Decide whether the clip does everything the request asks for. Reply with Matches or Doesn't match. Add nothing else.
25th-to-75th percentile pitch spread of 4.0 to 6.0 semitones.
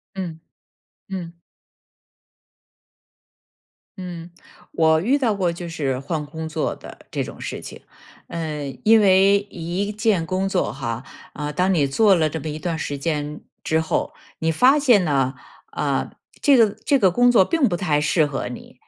Matches